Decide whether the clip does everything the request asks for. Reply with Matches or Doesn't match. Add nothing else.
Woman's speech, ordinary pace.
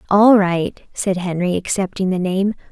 Matches